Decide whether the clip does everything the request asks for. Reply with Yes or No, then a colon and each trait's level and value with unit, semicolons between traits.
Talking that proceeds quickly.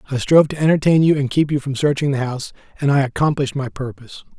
Yes: fast, 235 wpm